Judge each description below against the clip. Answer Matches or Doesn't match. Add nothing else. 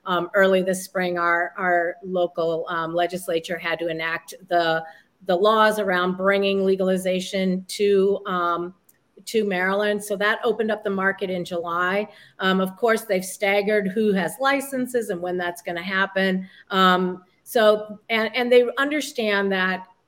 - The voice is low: Doesn't match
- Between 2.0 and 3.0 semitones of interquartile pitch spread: Matches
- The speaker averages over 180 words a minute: Doesn't match